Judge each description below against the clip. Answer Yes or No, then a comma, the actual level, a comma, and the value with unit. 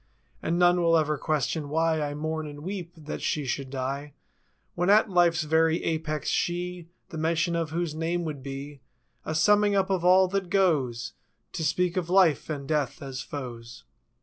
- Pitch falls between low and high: Yes, medium, 160 Hz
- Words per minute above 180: No, average, 175 wpm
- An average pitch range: Yes, average, 3.2 semitones